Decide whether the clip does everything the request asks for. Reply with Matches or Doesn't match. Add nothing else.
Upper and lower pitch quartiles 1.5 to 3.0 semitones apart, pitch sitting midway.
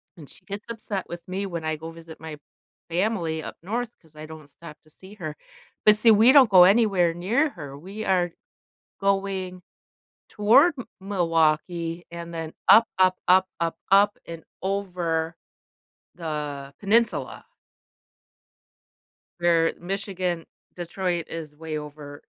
Doesn't match